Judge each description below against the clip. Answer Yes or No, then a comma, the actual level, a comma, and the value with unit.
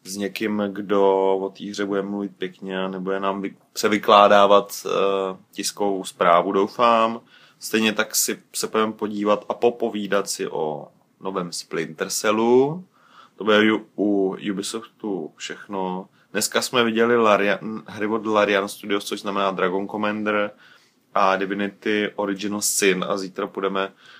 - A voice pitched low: Yes, low, 100 Hz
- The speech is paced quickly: No, average, 135 wpm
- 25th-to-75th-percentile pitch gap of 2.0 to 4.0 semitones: No, narrow, 1.6 semitones